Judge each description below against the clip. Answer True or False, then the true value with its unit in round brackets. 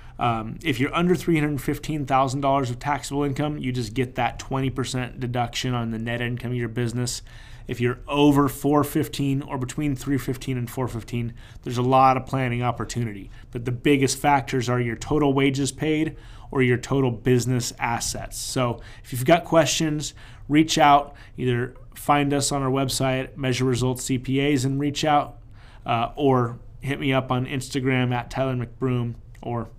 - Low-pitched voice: True (130 Hz)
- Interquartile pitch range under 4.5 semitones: True (2.7 semitones)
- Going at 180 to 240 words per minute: False (160 wpm)